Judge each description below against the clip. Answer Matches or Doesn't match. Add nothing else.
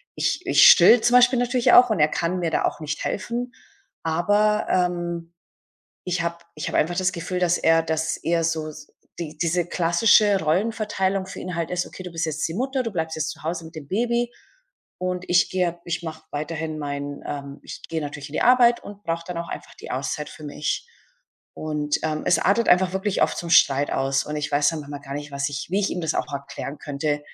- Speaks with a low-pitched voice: Doesn't match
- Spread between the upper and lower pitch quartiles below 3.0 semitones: Doesn't match